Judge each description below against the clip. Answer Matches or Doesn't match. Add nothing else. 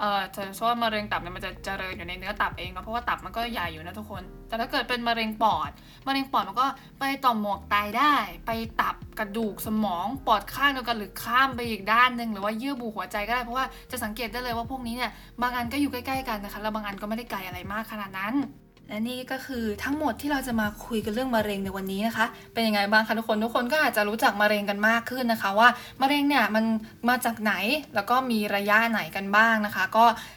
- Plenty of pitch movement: Doesn't match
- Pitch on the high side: Matches